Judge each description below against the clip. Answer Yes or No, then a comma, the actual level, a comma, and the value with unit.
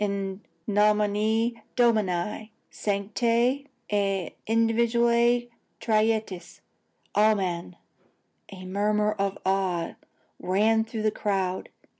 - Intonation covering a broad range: No, narrow, 2.5 semitones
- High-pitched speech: Yes, high, 210 Hz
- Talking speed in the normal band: No, slow, 80 wpm